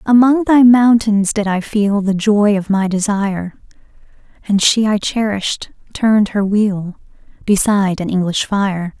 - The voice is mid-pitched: No, high, 205 Hz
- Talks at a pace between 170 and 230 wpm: No, average, 145 wpm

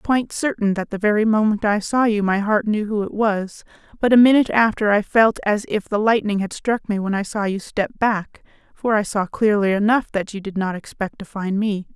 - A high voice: Yes, high, 210 Hz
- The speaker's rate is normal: No, fast, 240 wpm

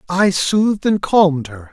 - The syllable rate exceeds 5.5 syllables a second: No, 4.6 syllables/s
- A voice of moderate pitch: Yes, medium, 175 Hz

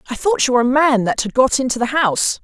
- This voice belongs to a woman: Yes, female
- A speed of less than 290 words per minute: No, fast, 295 wpm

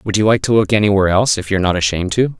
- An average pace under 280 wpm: No, fast, 300 wpm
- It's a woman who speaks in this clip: No, male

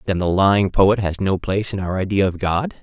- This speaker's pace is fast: Yes, fast, 255 wpm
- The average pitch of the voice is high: No, very low, 95 Hz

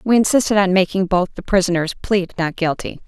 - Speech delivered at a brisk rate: No, average, 195 wpm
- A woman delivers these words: Yes, female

